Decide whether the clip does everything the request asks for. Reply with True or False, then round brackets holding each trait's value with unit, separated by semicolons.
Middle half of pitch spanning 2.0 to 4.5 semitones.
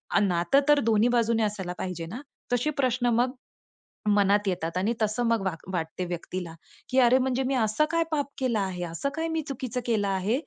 False (5.6 semitones)